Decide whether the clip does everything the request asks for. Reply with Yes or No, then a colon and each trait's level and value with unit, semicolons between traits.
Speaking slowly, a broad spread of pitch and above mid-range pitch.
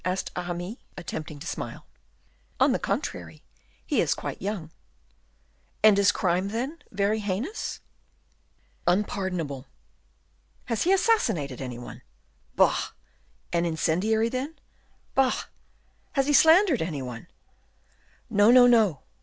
Yes: slow, 110 wpm; wide, 6.6 semitones; high, 200 Hz